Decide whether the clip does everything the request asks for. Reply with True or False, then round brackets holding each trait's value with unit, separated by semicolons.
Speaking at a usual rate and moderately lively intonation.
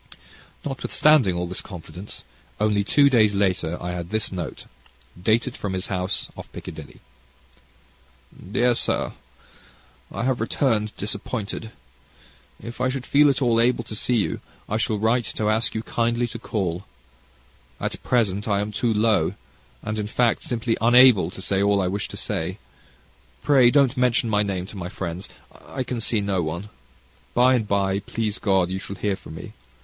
True (170 wpm; 3.8 semitones)